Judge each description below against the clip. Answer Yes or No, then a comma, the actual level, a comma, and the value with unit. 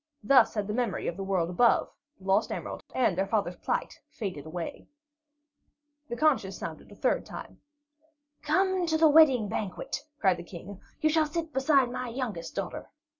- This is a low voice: No, high, 230 Hz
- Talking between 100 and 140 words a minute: No, average, 175 wpm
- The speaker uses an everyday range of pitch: No, wide, 7.4 semitones